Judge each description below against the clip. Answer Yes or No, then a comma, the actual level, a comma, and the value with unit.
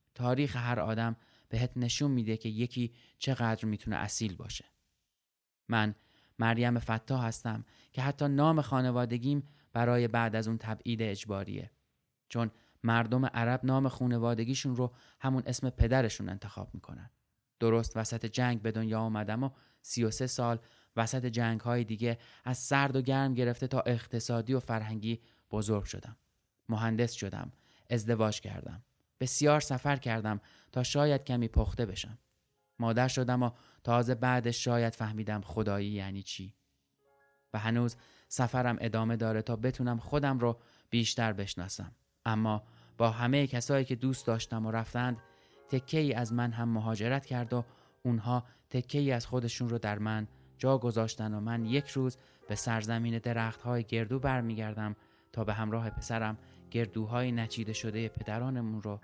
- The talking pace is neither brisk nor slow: Yes, average, 145 wpm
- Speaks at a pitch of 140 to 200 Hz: No, low, 115 Hz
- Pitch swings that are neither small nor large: No, narrow, 2.3 semitones